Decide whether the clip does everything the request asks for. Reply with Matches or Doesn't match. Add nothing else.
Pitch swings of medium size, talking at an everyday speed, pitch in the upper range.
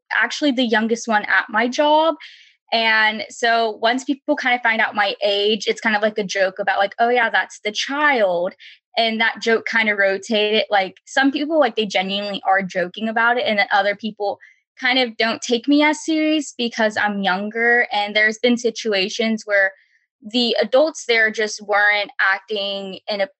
Matches